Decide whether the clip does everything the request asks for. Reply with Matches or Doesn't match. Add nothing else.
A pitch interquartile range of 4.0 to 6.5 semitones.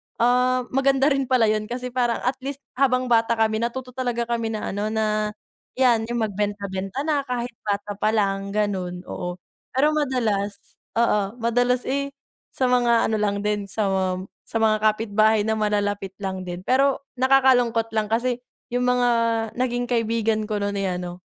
Doesn't match